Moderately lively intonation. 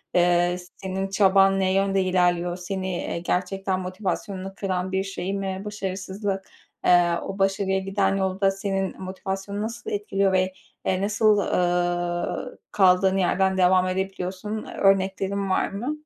No: narrow, 1.1 semitones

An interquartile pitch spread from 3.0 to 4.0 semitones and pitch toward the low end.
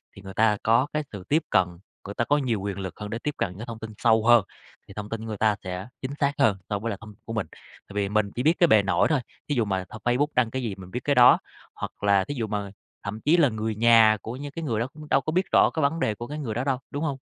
No: average, 4.8 semitones; low, 115 Hz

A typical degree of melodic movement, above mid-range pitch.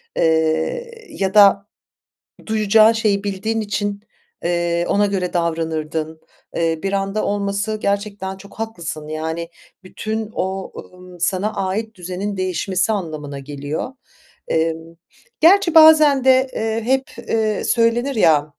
Yes: average, 4.7 semitones; high, 195 Hz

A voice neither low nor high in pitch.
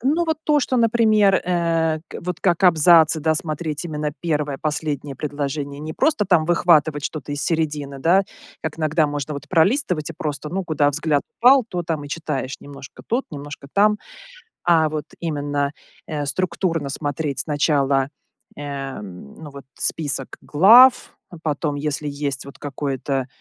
Yes: medium, 155 Hz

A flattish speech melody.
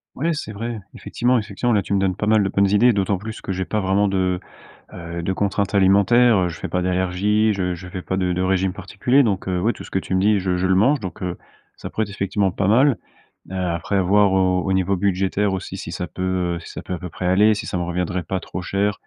Yes: narrow, 2.2 semitones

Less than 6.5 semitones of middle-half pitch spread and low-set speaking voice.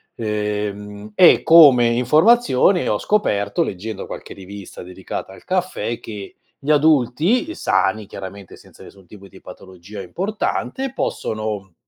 No: wide, 7.7 semitones; low, 110 Hz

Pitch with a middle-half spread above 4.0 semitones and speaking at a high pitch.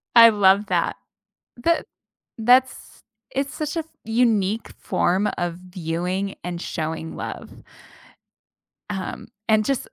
Yes: average, 4.9 semitones; high, 205 Hz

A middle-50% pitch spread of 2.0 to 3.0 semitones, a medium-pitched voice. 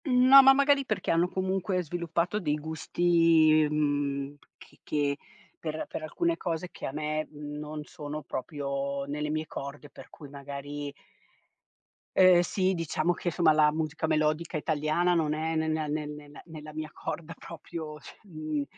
Yes: narrow, 2.4 semitones; medium, 155 Hz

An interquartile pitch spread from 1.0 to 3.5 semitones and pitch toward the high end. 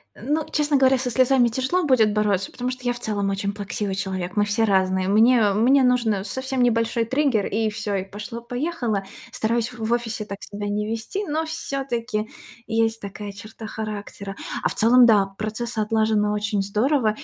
Yes: average, 3.2 semitones; high, 220 Hz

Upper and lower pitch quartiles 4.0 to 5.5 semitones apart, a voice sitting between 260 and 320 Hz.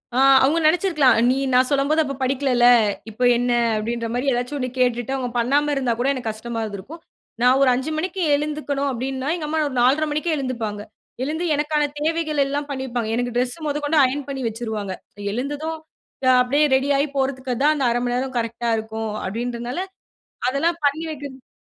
No: average, 3.3 semitones; very high, 265 Hz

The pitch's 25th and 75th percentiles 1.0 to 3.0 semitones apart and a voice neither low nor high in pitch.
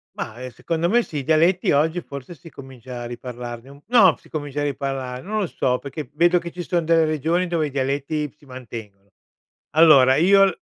No: average, 4.6 semitones; medium, 145 Hz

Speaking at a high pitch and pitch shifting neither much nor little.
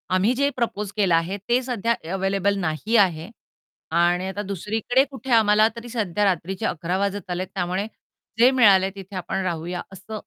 Yes: high, 195 Hz; average, 3.3 semitones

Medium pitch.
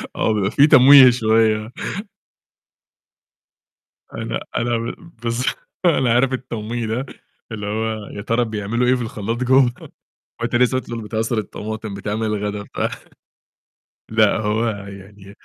No: low, 110 Hz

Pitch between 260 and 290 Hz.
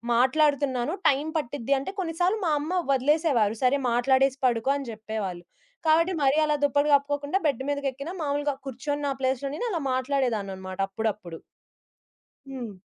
Yes: very high, 275 Hz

